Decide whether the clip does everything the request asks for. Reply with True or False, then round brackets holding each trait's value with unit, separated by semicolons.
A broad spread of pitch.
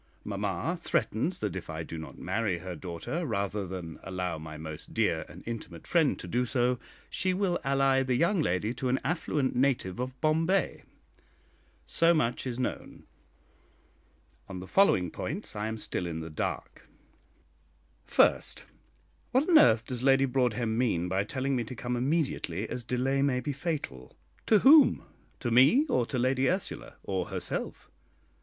True (6.5 semitones)